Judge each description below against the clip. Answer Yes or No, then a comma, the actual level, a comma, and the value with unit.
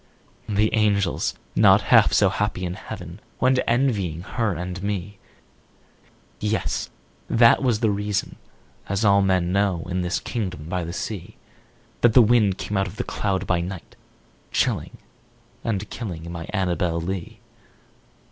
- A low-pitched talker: Yes, low, 100 Hz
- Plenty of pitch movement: No, average, 3.1 semitones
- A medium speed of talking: Yes, average, 145 wpm